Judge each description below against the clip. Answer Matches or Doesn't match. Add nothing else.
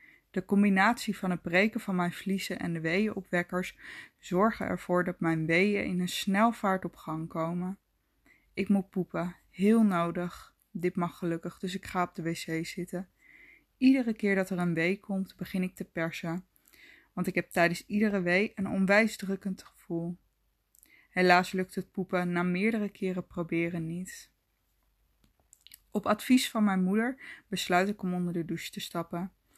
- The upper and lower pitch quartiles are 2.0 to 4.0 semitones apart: Matches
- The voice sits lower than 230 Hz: Matches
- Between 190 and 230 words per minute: Doesn't match